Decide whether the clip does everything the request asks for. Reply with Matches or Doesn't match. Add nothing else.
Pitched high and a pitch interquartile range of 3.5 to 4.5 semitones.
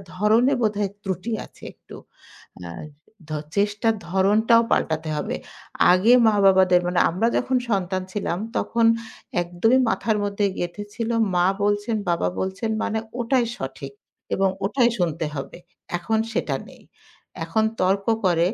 Matches